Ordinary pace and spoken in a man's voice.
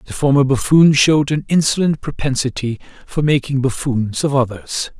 Yes: average, 145 wpm; male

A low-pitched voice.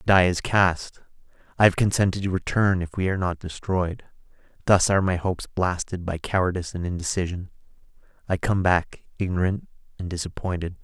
Yes: very low, 90 Hz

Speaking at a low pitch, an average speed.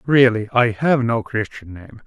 Yes: low, 120 Hz; average, 175 wpm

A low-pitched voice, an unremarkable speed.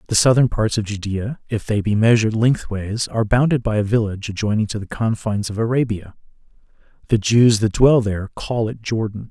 Yes: low, 110 Hz; average, 185 wpm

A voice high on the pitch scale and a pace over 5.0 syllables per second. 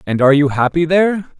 No: medium, 155 Hz; 6.7 syllables/s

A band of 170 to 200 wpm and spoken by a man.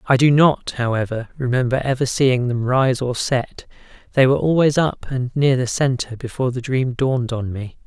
Yes: average, 190 wpm; male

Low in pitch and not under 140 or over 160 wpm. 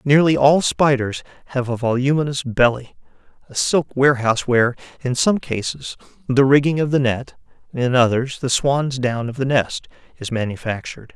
Yes: low, 130 Hz; average, 155 wpm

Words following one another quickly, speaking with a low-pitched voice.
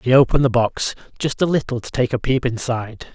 Yes: fast, 230 wpm; low, 125 Hz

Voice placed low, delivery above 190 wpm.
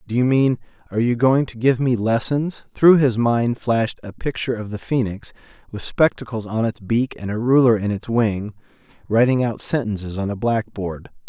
No: low, 115 Hz; average, 180 wpm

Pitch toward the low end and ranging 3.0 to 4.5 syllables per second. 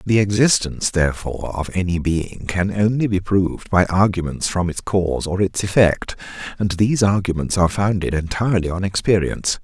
No: very low, 95 Hz; 5.5 syllables/s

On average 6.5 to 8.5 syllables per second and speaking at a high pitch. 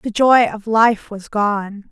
No: 3.3 syllables/s; high, 215 Hz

